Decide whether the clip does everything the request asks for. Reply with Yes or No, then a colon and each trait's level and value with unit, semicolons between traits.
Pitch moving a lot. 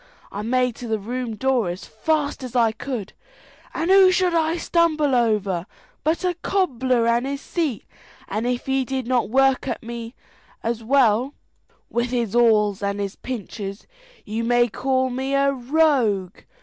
No: average, 3.8 semitones